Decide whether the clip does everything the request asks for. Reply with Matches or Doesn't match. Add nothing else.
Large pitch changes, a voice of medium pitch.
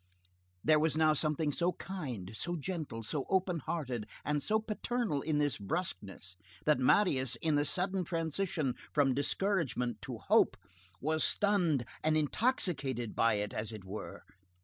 Matches